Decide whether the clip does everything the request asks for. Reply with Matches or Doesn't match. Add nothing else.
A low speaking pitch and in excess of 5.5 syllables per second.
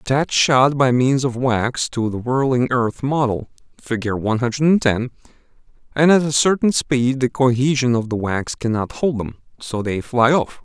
Doesn't match